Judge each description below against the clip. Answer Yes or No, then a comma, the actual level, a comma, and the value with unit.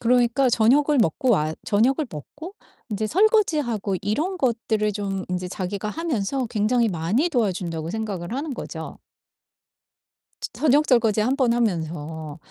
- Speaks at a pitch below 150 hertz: No, high, 220 Hz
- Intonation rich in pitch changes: Yes, wide, 5.7 semitones